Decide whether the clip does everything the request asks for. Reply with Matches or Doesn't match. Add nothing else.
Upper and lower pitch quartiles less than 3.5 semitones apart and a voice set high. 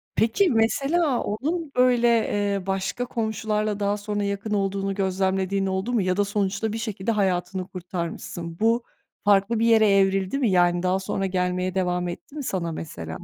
Matches